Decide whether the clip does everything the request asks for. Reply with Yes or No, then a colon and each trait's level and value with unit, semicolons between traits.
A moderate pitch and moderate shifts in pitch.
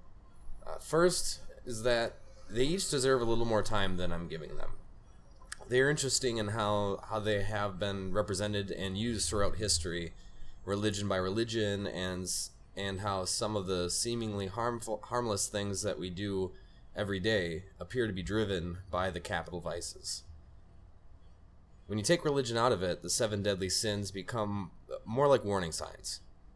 No: low, 100 Hz; average, 3.4 semitones